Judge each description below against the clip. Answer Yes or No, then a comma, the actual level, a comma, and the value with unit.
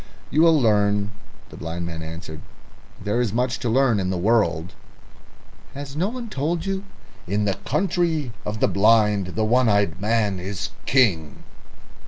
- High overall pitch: No, low, 110 Hz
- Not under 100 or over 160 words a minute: Yes, average, 155 wpm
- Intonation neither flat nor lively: No, wide, 6.1 semitones